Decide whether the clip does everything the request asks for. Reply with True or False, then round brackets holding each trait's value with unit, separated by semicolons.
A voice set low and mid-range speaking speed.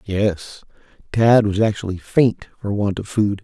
True (105 Hz; 155 wpm)